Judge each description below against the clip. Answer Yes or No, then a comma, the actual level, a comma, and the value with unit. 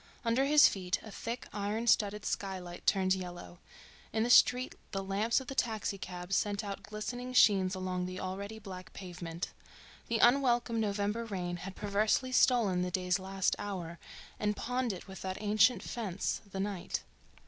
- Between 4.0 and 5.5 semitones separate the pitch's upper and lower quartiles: No, average, 3.4 semitones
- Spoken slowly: No, average, 165 wpm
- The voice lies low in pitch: No, high, 200 Hz